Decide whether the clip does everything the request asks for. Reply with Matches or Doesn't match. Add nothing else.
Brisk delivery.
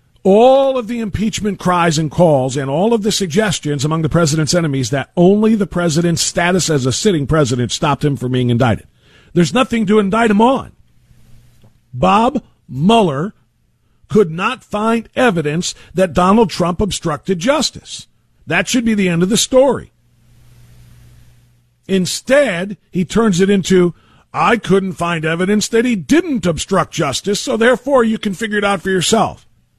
Doesn't match